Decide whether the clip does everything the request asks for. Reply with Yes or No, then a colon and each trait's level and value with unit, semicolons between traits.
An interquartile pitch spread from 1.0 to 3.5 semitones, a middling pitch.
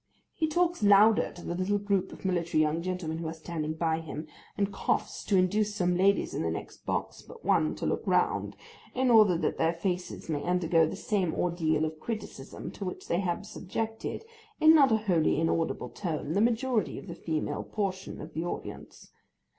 No: average, 4.1 semitones; medium, 180 Hz